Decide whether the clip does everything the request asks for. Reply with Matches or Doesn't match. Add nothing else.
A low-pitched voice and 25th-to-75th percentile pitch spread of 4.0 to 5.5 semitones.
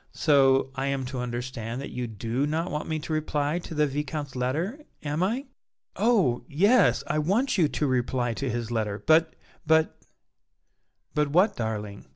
Doesn't match